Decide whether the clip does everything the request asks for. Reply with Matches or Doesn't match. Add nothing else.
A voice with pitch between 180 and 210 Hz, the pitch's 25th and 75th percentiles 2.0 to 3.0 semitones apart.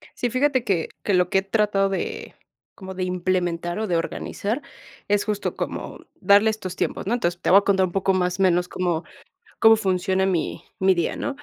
Matches